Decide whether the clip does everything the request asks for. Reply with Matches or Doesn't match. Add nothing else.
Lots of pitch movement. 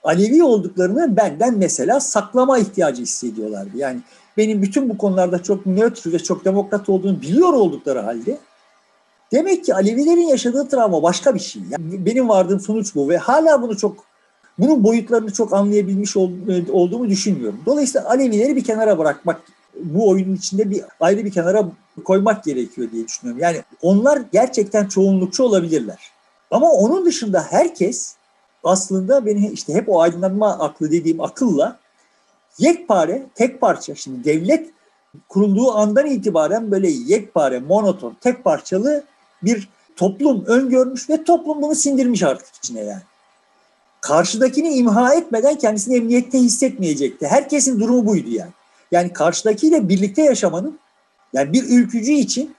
Matches